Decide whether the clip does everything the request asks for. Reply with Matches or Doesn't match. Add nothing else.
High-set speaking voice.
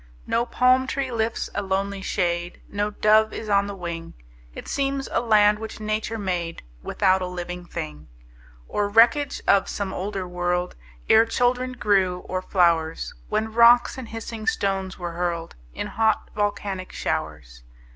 Matches